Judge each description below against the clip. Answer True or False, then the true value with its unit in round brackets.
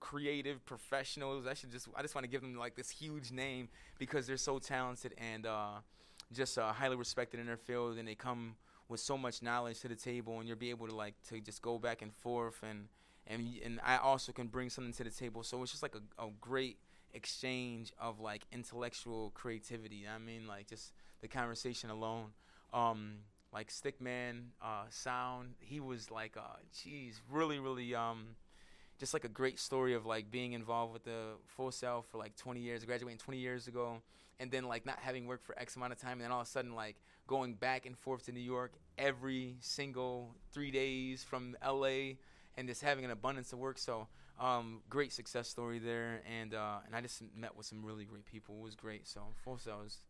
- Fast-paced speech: True (215 wpm)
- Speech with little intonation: True (2.3 semitones)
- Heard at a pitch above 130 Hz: False (120 Hz)